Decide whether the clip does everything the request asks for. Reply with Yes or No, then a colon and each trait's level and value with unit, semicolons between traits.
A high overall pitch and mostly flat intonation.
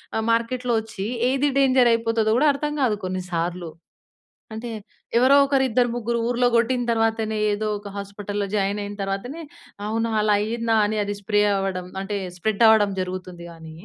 No: high, 220 Hz; average, 3.1 semitones